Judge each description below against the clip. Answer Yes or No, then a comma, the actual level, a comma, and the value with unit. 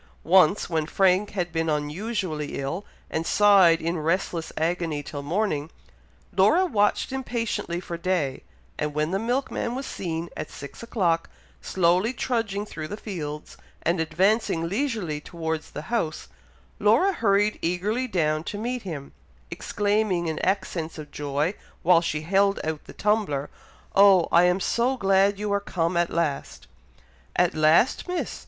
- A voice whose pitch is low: No, medium, 180 Hz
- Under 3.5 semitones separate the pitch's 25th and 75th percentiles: No, average, 4.4 semitones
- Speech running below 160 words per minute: Yes, average, 145 wpm